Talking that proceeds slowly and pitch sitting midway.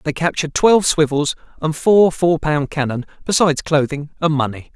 No: average, 165 wpm; medium, 155 Hz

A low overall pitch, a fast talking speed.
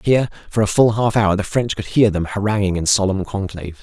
Yes: low, 100 Hz; fast, 235 wpm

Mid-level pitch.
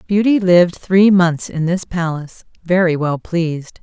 Yes: medium, 175 Hz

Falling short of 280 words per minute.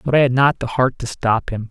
No: fast, 315 wpm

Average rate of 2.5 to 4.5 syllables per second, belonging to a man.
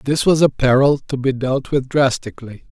No: 5.1 syllables/s; male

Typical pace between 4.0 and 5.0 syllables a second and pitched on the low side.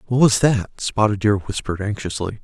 No: 5.3 syllables/s; low, 105 Hz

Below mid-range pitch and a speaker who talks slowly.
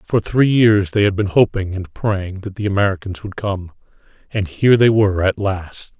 No: low, 100 Hz; average, 190 wpm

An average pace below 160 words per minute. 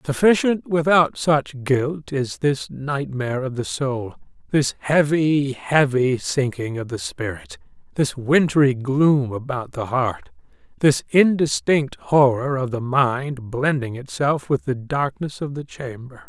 Yes: slow, 135 wpm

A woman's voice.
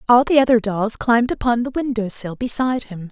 Yes: female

